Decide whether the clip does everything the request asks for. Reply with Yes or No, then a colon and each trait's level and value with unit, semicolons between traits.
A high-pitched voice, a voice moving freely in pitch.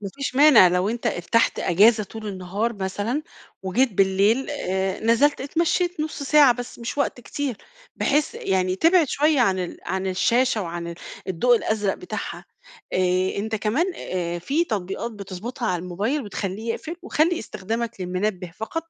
Yes: high, 215 Hz; wide, 6.1 semitones